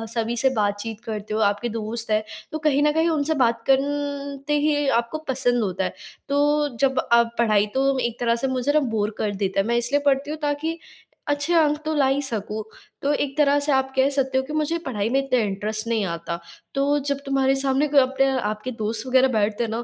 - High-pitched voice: Yes, very high, 265 Hz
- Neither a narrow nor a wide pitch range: Yes, average, 4.5 semitones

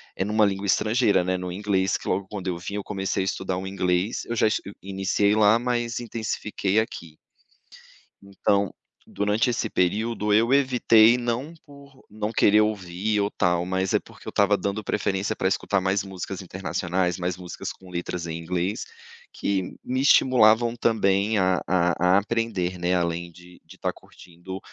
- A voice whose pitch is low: Yes, low, 100 Hz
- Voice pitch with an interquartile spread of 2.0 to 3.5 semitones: Yes, average, 3.1 semitones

